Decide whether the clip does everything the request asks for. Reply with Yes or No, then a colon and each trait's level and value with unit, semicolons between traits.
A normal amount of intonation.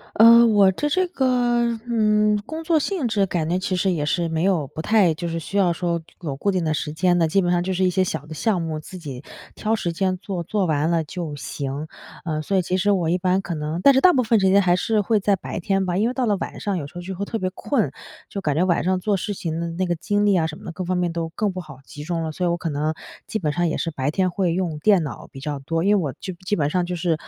Yes: average, 3.7 semitones